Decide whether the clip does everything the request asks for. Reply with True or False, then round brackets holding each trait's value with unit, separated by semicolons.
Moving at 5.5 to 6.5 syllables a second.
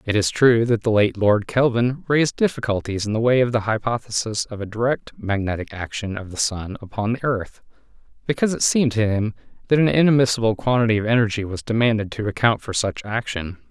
True (5.9 syllables/s)